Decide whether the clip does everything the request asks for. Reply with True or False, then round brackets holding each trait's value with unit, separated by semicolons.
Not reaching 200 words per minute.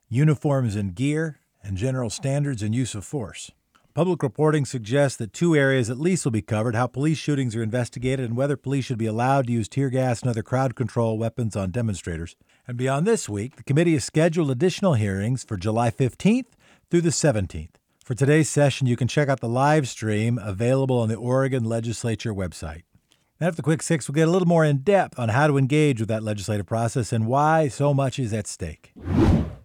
False (205 wpm)